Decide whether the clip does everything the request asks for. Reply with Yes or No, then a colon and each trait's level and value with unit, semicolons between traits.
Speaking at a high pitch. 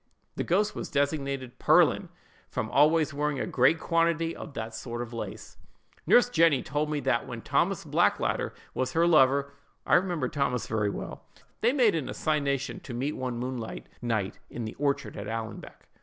No: medium, 140 Hz